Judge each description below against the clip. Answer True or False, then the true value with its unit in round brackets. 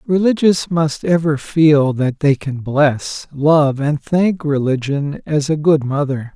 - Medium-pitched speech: True (150 Hz)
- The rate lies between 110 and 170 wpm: True (150 wpm)